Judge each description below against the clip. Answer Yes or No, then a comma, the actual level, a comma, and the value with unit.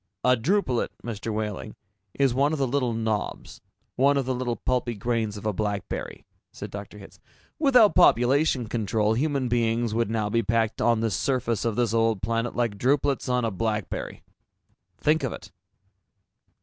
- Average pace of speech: Yes, average, 165 wpm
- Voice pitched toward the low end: Yes, low, 115 Hz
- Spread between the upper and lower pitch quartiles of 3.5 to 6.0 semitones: No, average, 2.9 semitones